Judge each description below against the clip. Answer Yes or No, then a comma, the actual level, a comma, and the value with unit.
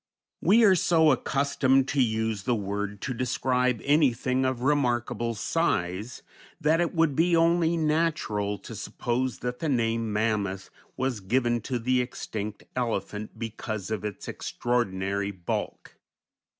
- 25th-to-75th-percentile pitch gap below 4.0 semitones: No, average, 4.7 semitones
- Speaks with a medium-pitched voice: No, low, 120 Hz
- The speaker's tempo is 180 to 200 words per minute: No, slow, 135 wpm